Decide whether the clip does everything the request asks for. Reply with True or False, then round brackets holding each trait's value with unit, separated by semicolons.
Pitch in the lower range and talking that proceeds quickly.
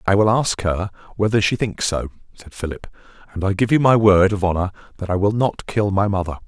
True (100 Hz; 230 wpm)